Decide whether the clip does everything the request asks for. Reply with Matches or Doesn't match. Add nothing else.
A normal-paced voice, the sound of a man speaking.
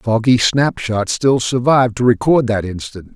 Matches